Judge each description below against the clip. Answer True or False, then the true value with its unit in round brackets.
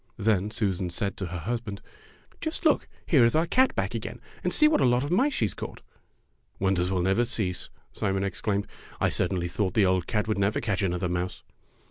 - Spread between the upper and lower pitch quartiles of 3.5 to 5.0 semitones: True (3.9 semitones)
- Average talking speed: False (215 wpm)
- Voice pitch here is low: True (100 Hz)